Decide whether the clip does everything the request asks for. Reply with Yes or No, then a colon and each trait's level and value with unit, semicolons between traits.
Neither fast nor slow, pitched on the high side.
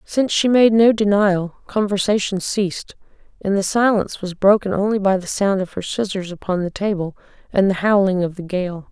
Yes: average, 190 wpm; high, 195 Hz